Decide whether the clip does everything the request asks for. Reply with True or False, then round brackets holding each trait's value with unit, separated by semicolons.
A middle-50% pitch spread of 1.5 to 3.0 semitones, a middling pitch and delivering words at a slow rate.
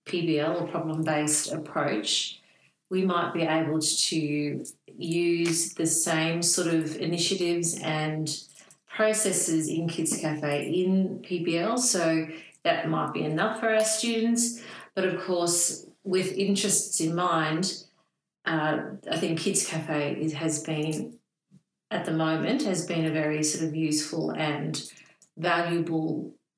True (2.7 semitones; 165 Hz; 130 wpm)